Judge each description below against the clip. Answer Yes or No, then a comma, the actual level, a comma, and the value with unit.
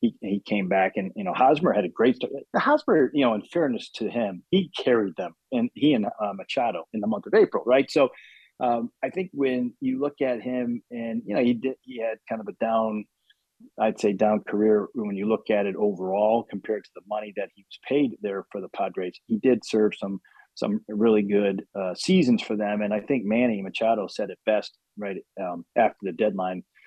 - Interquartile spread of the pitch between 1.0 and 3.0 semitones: No, average, 3.5 semitones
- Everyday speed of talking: No, fast, 220 wpm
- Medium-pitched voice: No, low, 110 Hz